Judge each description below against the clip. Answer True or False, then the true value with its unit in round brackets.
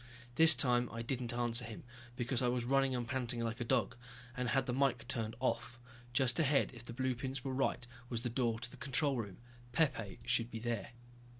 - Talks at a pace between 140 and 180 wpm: False (205 wpm)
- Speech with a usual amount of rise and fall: False (2.2 semitones)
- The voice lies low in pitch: True (120 Hz)